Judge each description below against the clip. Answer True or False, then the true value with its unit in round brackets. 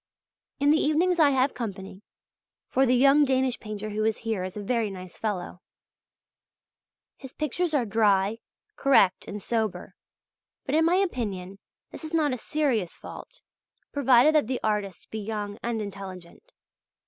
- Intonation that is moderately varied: False (5.8 semitones)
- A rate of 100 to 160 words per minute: True (155 wpm)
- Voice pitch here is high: True (230 Hz)